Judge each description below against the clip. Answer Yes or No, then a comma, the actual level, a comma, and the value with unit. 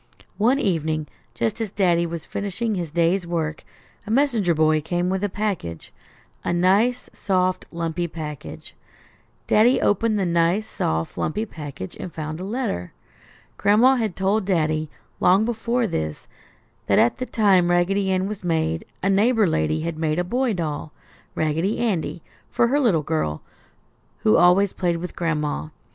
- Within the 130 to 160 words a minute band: Yes, average, 155 wpm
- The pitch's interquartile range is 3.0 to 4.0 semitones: No, average, 4.7 semitones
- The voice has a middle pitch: Yes, medium, 180 Hz